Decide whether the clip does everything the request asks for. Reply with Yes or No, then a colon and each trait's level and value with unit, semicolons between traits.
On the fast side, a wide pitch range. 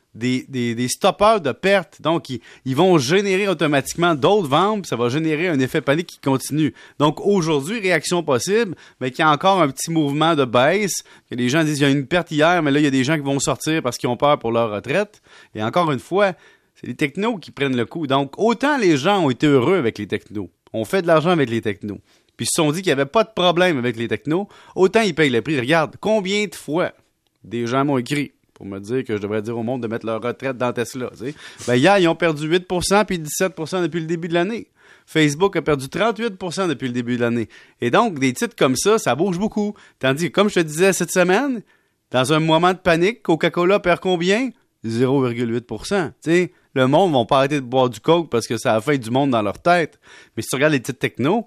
Yes: fast, 245 wpm; wide, 6.0 semitones